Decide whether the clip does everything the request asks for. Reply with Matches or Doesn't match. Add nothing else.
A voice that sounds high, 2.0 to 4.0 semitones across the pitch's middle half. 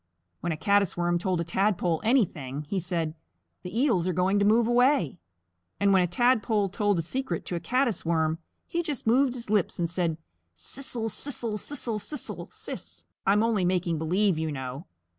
Doesn't match